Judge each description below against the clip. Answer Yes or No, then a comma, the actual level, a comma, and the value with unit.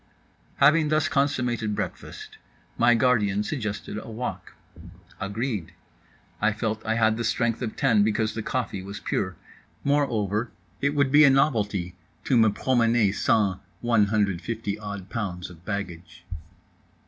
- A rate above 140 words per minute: No, slow, 135 wpm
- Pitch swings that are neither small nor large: Yes, average, 3.6 semitones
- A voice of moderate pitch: No, low, 110 Hz